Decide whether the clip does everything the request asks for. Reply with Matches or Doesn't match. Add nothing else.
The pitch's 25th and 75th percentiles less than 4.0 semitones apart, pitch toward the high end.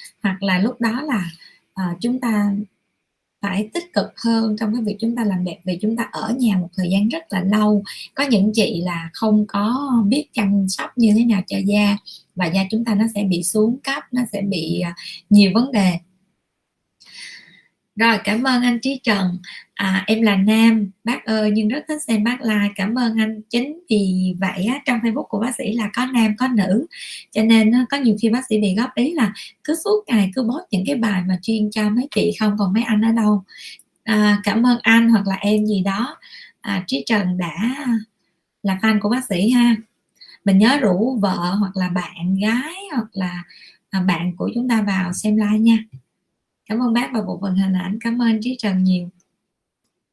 Matches